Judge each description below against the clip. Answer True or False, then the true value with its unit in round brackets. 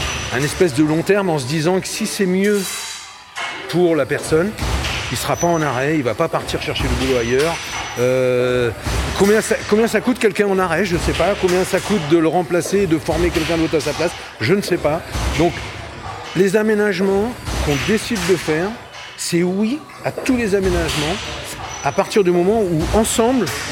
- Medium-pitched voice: True (180 Hz)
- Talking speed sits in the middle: True (195 wpm)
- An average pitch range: True (4.1 semitones)